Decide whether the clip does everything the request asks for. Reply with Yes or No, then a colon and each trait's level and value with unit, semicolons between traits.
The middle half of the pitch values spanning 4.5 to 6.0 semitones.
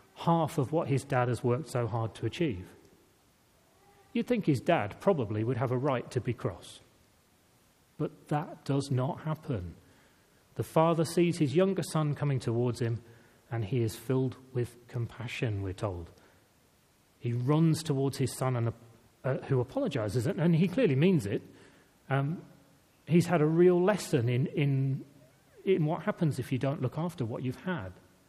Yes: average, 4.8 semitones